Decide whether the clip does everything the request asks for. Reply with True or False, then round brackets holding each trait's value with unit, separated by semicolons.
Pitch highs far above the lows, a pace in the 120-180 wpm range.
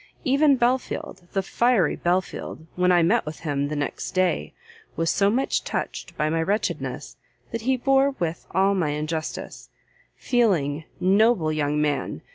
True (7.1 semitones; 150 wpm)